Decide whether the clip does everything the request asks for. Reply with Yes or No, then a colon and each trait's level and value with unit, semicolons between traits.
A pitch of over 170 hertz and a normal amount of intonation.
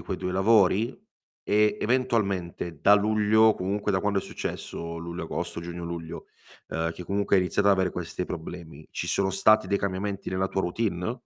No: very low, 95 Hz; average, 3.1 semitones